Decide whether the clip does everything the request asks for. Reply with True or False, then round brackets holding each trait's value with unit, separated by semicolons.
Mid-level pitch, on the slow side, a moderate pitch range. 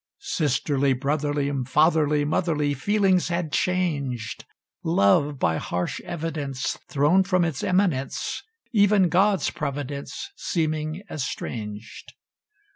True (150 Hz; 95 wpm; 4.3 semitones)